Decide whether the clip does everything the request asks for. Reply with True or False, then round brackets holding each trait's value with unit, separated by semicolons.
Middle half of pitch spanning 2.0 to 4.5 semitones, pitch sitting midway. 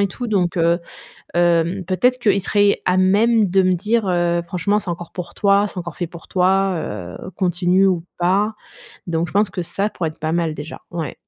True (2.7 semitones; 180 Hz)